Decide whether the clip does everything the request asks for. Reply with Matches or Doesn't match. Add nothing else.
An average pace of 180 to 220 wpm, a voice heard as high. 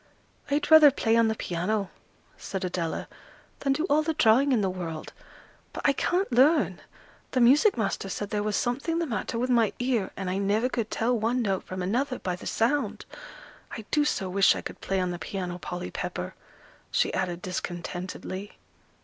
Matches